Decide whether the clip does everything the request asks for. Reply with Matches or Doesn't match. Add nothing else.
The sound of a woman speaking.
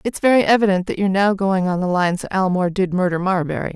Matches